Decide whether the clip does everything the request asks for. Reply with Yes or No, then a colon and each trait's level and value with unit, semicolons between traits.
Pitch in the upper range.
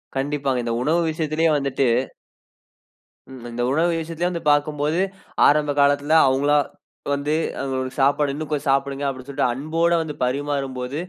No: medium, 145 Hz